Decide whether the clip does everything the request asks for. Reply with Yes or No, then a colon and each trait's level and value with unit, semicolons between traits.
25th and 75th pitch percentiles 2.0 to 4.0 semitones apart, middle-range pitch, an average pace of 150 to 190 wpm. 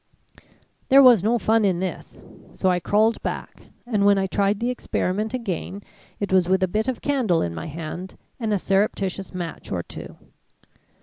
No: average, 3.3 semitones; high, 200 Hz; average, 180 wpm